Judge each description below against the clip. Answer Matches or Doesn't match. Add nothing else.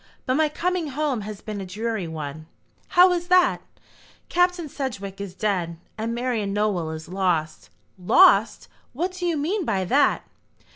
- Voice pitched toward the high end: Matches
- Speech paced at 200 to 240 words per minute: Doesn't match